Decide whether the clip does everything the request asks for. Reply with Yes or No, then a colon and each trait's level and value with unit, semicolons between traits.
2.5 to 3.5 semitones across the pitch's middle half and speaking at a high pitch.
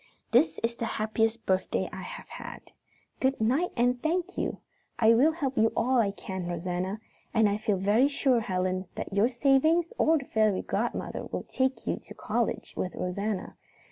No: average, 5.2 semitones; high, 225 Hz